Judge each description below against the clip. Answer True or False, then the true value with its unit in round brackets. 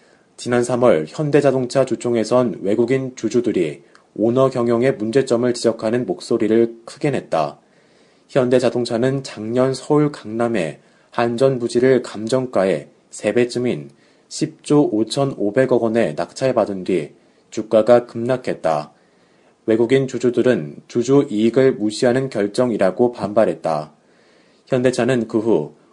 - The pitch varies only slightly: True (2.3 semitones)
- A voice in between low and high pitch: False (120 Hz)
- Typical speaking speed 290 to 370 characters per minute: False (260 characters per minute)